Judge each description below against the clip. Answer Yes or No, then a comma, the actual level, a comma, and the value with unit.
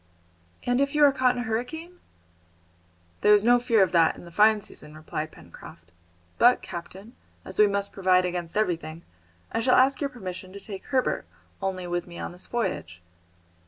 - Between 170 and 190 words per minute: Yes, average, 185 wpm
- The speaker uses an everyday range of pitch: No, wide, 5.7 semitones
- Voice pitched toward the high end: Yes, high, 200 Hz